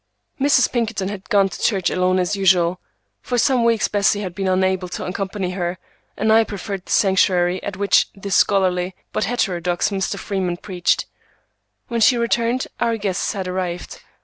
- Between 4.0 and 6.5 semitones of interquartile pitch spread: No, average, 2.8 semitones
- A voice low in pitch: No, high, 195 Hz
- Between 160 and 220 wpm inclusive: Yes, average, 170 wpm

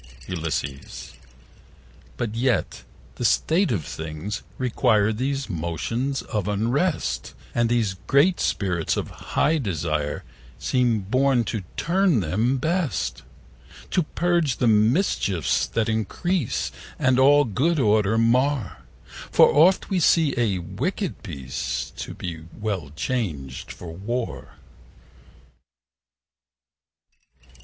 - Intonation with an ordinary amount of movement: No, wide, 8.0 semitones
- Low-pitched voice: Yes, low, 110 Hz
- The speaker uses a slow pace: Yes, slow, 105 wpm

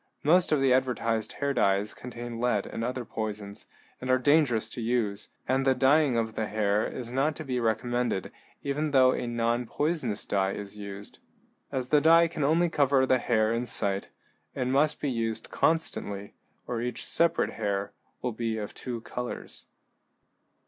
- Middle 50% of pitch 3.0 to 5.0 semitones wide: Yes, average, 3.7 semitones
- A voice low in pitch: Yes, low, 120 Hz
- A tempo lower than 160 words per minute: No, average, 170 wpm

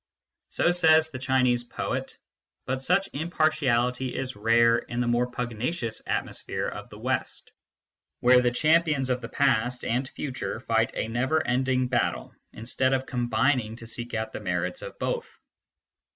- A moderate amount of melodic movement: No, narrow, 2.1 semitones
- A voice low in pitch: Yes, low, 125 Hz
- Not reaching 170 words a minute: Yes, average, 150 wpm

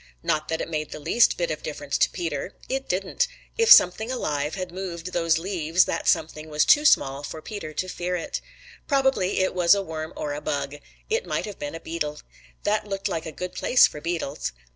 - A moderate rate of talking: No, fast, 210 wpm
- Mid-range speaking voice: Yes, medium, 170 Hz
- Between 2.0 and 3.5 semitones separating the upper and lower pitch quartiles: No, average, 4.1 semitones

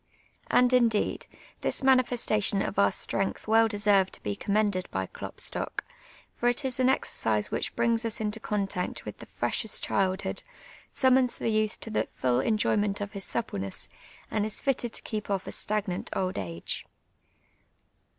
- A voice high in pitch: Yes, high, 210 Hz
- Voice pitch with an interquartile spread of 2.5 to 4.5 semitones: Yes, average, 3.2 semitones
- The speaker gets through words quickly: No, average, 160 wpm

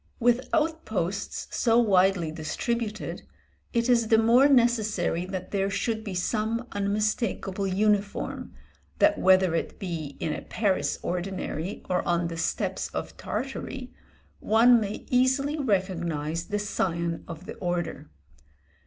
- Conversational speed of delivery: No, slow, 125 wpm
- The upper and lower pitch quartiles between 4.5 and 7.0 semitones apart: Yes, average, 4.8 semitones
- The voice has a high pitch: Yes, high, 200 Hz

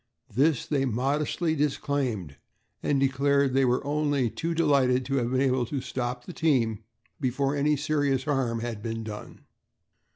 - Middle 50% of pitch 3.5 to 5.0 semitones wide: No, average, 2.8 semitones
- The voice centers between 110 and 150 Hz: Yes, low, 135 Hz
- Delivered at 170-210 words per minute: No, average, 155 wpm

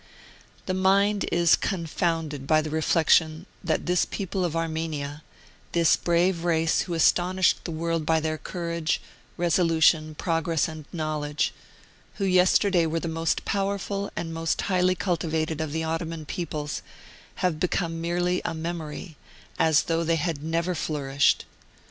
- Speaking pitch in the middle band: Yes, medium, 165 Hz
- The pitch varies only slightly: Yes, narrow, 2.0 semitones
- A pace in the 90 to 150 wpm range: Yes, average, 140 wpm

